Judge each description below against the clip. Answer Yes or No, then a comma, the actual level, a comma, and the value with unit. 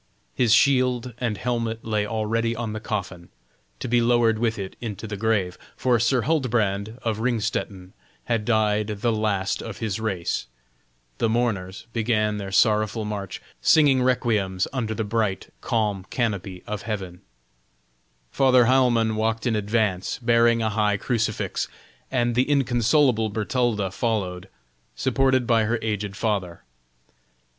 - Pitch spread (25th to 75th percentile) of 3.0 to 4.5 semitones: No, narrow, 2.5 semitones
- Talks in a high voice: No, low, 110 Hz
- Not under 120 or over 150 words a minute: Yes, slow, 135 wpm